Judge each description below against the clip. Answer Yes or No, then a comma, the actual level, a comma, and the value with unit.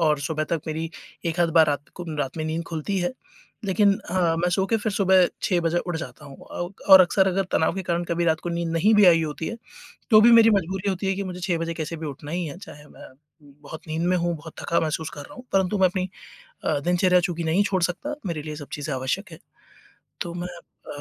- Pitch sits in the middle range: Yes, medium, 170 Hz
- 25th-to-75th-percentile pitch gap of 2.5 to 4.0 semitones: Yes, average, 2.9 semitones